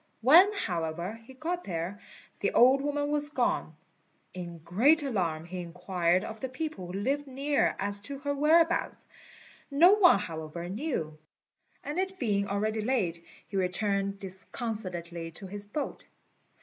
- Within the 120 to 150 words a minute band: Yes, average, 145 wpm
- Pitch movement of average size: No, wide, 8.0 semitones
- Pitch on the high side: Yes, high, 210 Hz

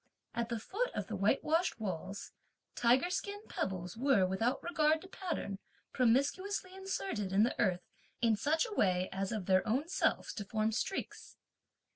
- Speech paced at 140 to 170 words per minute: Yes, average, 165 wpm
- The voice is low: No, high, 230 Hz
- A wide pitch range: Yes, wide, 8.8 semitones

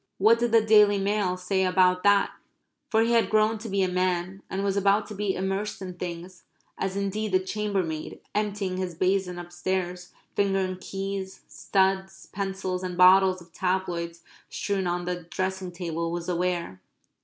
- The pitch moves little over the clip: Yes, narrow, 1.7 semitones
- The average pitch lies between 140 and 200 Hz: Yes, high, 190 Hz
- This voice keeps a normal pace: Yes, average, 165 wpm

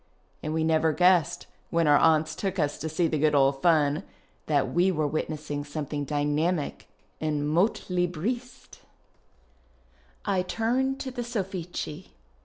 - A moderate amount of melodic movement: Yes, average, 3.5 semitones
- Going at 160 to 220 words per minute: No, slow, 135 wpm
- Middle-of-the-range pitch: Yes, medium, 160 Hz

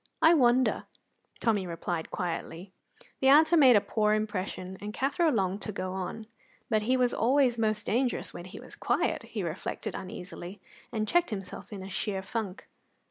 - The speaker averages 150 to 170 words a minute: Yes, average, 165 wpm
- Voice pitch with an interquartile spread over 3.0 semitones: Yes, average, 4.7 semitones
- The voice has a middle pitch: No, high, 210 Hz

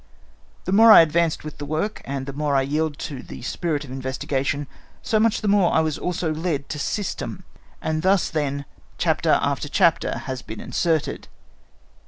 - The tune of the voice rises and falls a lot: No, average, 3.8 semitones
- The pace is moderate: Yes, average, 180 wpm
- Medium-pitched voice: Yes, medium, 155 Hz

